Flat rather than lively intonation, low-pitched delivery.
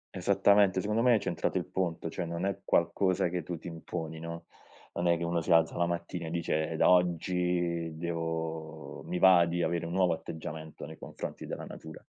Yes: narrow, 1.6 semitones; very low, 85 Hz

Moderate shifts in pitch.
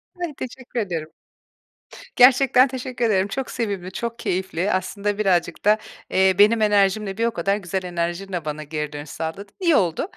Yes: average, 4.7 semitones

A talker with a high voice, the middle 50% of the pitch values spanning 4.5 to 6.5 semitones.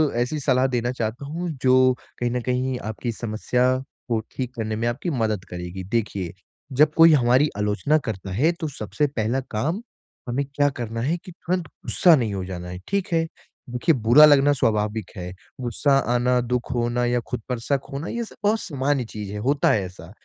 No: low, 125 Hz; average, 4.8 semitones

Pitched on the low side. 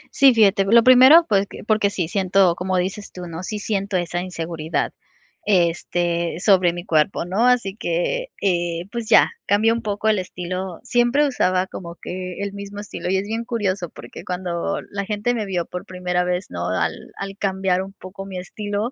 No: high, 190 Hz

